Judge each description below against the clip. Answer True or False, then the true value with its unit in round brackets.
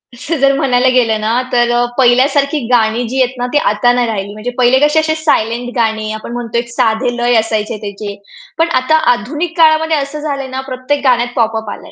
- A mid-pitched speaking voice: False (245 Hz)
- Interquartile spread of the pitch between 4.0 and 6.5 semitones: False (3.5 semitones)